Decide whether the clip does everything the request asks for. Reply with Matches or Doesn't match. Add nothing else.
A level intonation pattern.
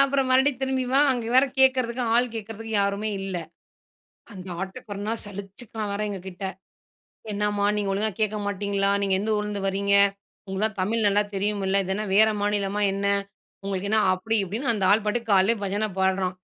Matches